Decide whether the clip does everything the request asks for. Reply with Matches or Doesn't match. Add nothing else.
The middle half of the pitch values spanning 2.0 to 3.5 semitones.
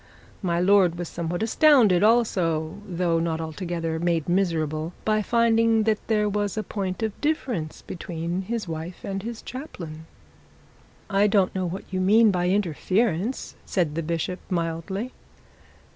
Doesn't match